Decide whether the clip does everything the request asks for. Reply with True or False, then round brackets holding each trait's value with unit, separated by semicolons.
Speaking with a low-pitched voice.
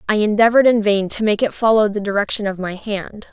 False (210 Hz)